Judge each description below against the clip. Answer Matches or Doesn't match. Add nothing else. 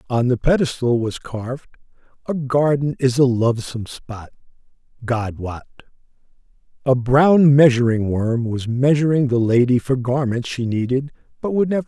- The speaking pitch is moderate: Doesn't match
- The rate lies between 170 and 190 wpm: Doesn't match